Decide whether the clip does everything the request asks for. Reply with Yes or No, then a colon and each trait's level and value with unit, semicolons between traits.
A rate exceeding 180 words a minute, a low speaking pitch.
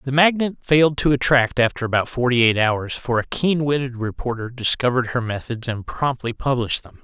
Yes: average, 190 wpm; low, 125 Hz